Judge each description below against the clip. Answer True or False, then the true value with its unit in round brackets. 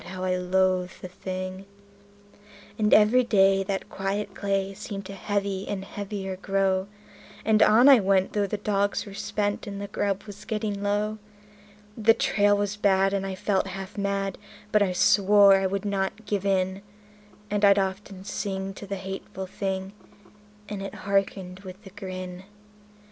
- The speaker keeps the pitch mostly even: True (1.2 semitones)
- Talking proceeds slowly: False (165 wpm)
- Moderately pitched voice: False (195 Hz)